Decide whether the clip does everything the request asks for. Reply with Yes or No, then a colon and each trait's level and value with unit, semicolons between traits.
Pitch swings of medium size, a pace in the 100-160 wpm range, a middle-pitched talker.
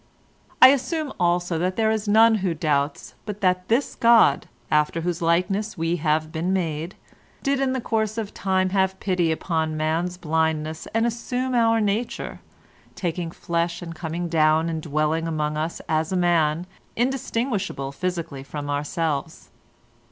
Yes: average, 4.8 semitones; average, 150 wpm; medium, 175 Hz